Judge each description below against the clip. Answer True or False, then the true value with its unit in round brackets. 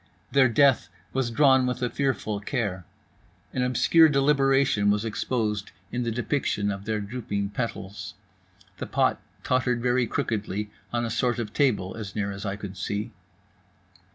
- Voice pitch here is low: True (115 Hz)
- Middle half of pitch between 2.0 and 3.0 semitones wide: False (3.8 semitones)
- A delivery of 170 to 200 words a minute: False (155 wpm)